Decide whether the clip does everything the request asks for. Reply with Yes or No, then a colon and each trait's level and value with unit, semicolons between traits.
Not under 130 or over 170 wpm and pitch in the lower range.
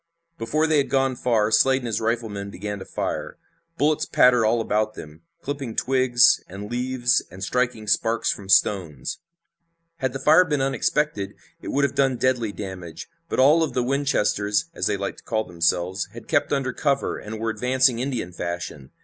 No: average, 180 wpm; low, 120 Hz